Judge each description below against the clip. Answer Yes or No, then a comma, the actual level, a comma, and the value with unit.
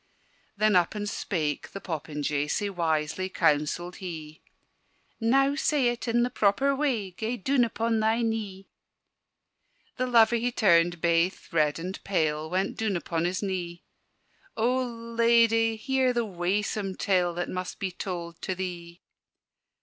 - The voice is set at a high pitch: Yes, high, 195 Hz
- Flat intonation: No, average, 5.1 semitones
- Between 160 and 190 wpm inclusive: No, average, 140 wpm